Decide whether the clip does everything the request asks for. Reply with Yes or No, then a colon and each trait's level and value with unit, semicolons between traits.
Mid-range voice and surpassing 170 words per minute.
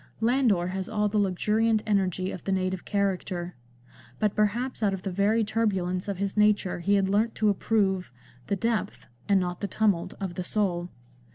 No: high, 200 Hz; average, 180 wpm